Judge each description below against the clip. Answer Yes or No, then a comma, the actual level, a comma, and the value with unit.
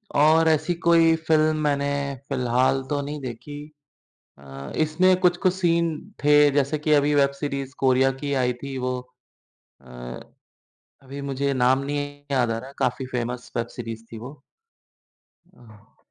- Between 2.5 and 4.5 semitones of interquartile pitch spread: Yes, average, 3.2 semitones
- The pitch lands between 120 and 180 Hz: Yes, medium, 140 Hz